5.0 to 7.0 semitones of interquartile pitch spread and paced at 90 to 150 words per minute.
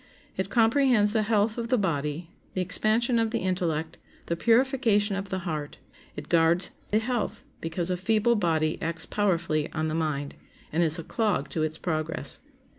No: wide, 5.4 semitones; average, 175 wpm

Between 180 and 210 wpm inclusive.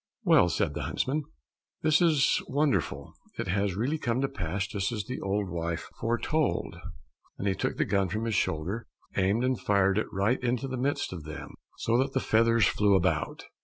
Yes: average, 185 wpm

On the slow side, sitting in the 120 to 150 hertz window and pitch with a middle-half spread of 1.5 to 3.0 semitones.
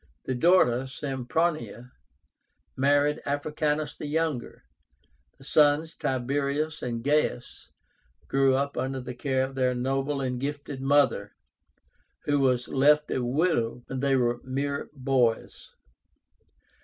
Yes: slow, 120 wpm; low, 135 Hz; narrow, 2.5 semitones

